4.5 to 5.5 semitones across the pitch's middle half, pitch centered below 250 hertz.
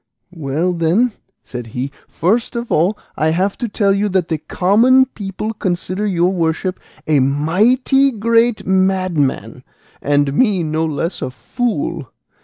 Yes: average, 5.2 semitones; medium, 185 Hz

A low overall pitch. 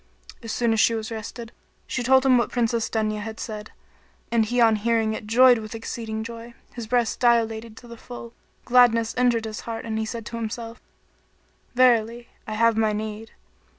No: high, 230 Hz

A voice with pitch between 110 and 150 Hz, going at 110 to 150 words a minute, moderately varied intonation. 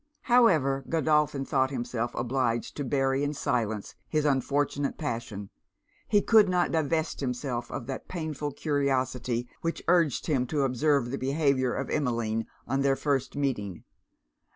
Yes: low, 135 Hz; average, 140 wpm; average, 3.3 semitones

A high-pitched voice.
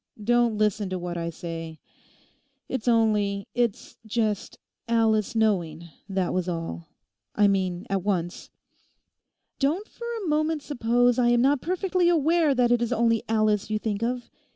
Yes: high, 220 Hz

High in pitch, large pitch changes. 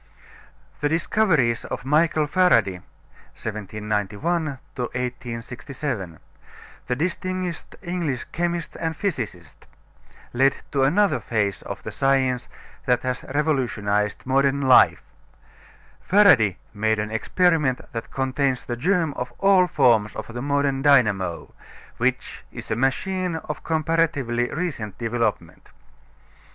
No: low, 135 Hz; wide, 5.8 semitones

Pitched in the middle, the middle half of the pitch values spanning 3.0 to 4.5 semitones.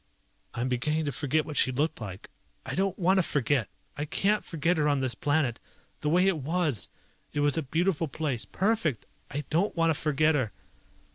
Yes: medium, 150 Hz; average, 3.7 semitones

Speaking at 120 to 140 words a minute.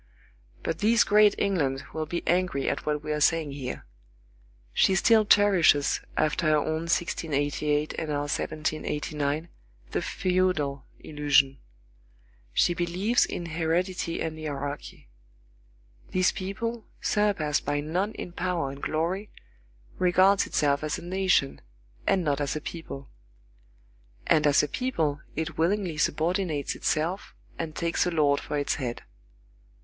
Yes: slow, 135 wpm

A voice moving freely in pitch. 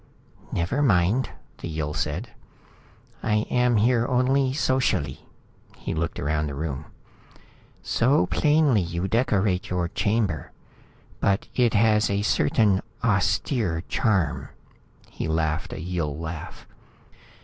Yes: wide, 6.1 semitones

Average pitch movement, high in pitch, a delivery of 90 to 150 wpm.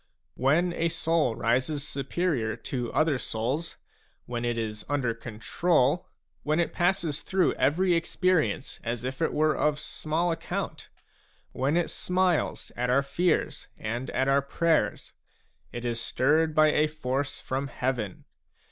No: average, 4.9 semitones; medium, 145 Hz; average, 140 wpm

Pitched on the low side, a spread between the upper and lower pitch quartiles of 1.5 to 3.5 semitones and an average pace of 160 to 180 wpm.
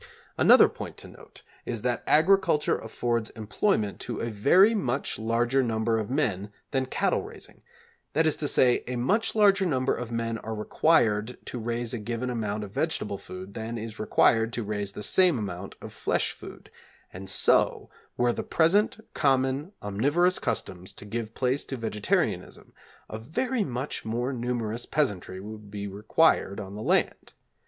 No: low, 120 Hz; average, 4.6 semitones; average, 165 wpm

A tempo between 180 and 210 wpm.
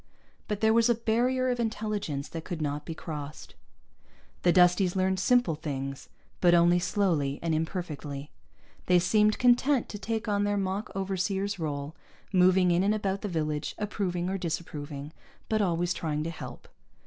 No: average, 160 wpm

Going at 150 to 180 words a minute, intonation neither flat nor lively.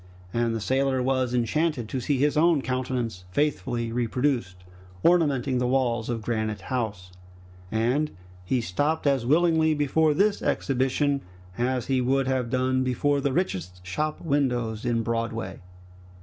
No: average, 140 wpm; average, 3.6 semitones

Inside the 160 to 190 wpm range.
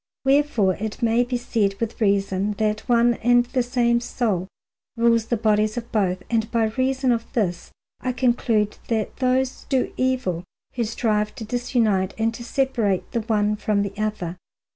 Yes: average, 165 wpm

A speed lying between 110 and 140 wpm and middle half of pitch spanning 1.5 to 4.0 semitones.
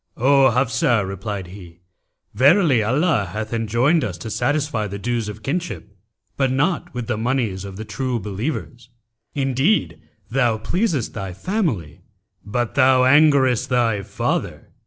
No: slow, 135 wpm; average, 4.8 semitones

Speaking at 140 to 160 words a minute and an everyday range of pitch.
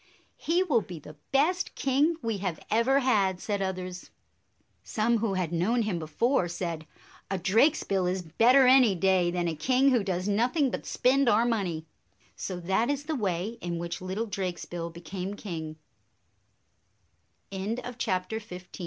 No: average, 150 wpm; wide, 5.7 semitones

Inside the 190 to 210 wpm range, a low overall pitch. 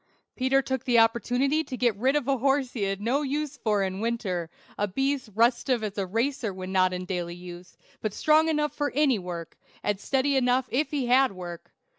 No: fast, 205 wpm; high, 240 Hz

